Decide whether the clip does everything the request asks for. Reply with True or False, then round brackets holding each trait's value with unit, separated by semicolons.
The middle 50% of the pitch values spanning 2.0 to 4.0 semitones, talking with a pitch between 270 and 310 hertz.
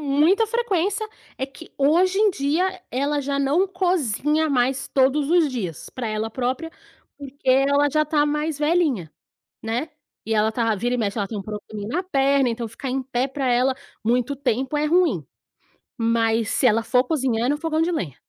False (4.7 semitones; 275 Hz)